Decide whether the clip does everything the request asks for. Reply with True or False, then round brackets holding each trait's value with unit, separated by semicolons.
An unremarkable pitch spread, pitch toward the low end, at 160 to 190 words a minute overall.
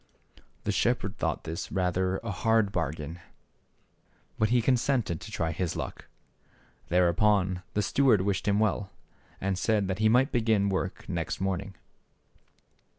True (3.3 semitones; 100 Hz; 170 wpm)